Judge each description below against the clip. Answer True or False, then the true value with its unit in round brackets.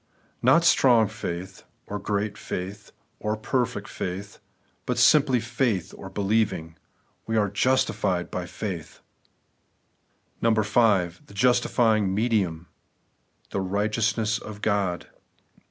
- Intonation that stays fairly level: False (3.0 semitones)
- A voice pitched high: False (105 Hz)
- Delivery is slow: True (105 wpm)